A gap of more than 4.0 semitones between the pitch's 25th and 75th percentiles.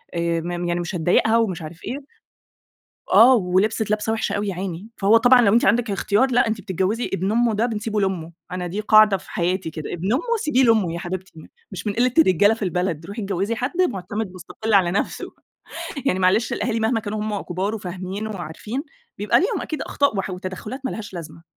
No: average, 3.7 semitones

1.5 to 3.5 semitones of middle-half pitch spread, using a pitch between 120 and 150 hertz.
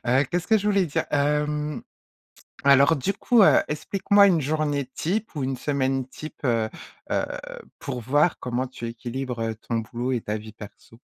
No: average, 4.3 semitones; medium, 140 Hz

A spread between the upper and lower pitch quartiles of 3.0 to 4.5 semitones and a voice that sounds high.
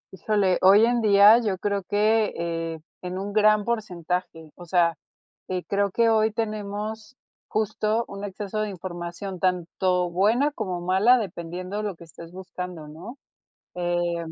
Yes: average, 3.3 semitones; high, 195 Hz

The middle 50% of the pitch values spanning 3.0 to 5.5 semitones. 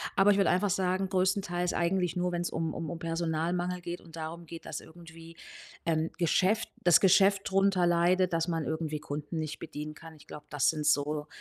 No: narrow, 2.4 semitones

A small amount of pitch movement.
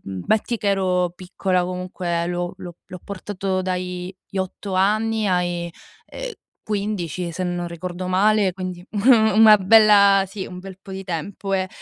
Yes: narrow, 2.1 semitones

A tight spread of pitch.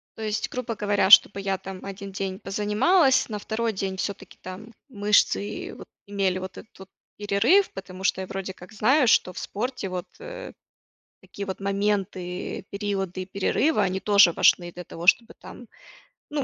Yes: narrow, 2.1 semitones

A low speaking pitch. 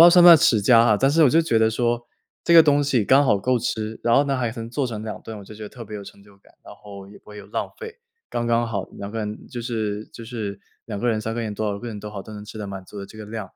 Yes: low, 110 Hz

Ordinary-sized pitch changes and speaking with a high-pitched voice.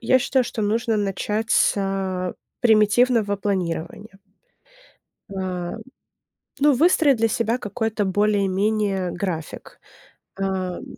Yes: average, 3.0 semitones; high, 205 Hz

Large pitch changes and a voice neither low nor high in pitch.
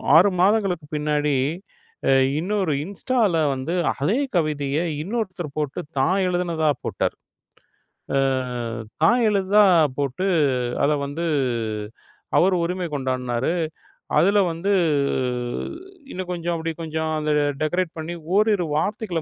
No: average, 4.1 semitones; medium, 170 Hz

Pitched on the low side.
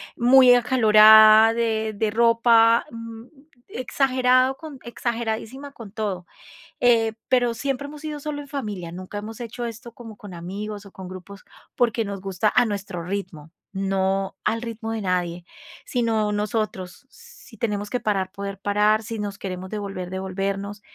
No: high, 215 Hz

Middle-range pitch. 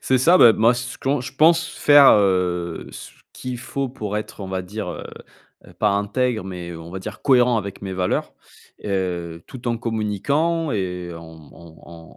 No: low, 105 Hz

